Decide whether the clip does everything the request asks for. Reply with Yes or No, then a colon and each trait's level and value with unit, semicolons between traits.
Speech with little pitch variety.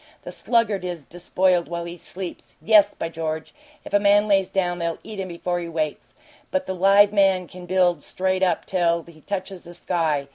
Yes: narrow, 2.3 semitones